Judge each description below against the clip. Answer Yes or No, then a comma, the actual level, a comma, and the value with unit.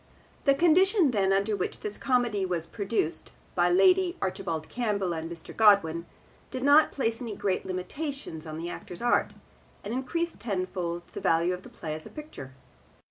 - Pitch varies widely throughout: Yes, wide, 7.0 semitones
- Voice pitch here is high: Yes, high, 200 Hz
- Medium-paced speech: Yes, average, 170 wpm